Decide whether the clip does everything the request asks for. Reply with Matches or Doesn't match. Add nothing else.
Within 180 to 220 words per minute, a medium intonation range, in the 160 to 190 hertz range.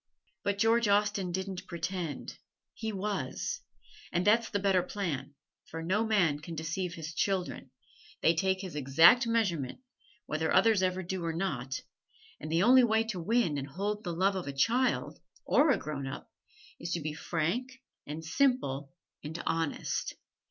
Doesn't match